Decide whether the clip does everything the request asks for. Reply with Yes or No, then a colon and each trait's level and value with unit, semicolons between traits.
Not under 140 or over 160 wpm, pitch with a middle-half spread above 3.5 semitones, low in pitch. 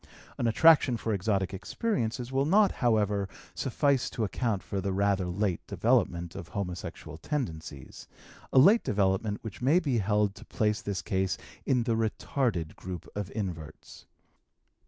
Yes: average, 145 wpm; average, 4.5 semitones; low, 105 Hz